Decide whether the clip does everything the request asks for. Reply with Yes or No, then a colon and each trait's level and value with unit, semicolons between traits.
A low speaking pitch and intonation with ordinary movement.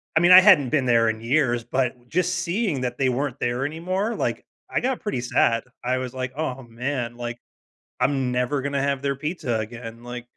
Yes: low, 130 Hz; average, 3.7 semitones